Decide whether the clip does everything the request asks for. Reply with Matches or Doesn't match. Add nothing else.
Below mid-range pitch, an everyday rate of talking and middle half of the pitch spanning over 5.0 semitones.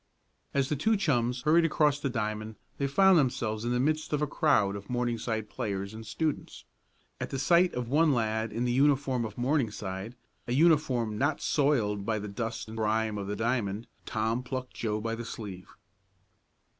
Doesn't match